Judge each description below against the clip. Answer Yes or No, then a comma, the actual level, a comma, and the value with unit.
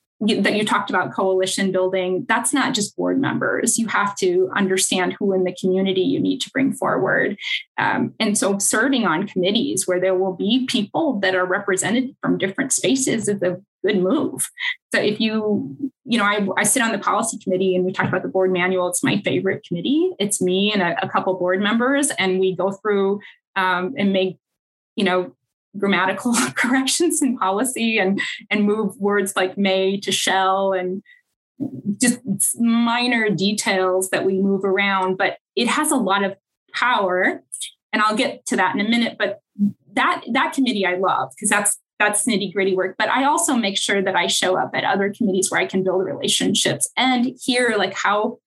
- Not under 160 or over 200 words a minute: Yes, average, 190 wpm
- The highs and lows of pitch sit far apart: No, average, 4.1 semitones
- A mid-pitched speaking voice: No, high, 205 Hz